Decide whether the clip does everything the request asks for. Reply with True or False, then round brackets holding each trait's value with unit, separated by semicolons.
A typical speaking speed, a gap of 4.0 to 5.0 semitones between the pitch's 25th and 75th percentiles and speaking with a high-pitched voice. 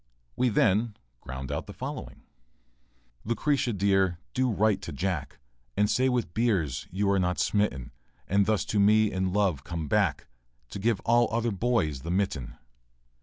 False (160 wpm; 4.3 semitones; 100 Hz)